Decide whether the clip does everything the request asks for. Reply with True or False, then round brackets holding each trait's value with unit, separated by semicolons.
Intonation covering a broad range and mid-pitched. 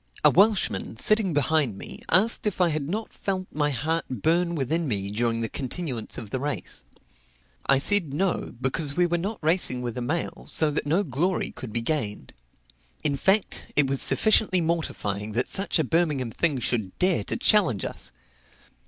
True (6.2 semitones; 150 Hz)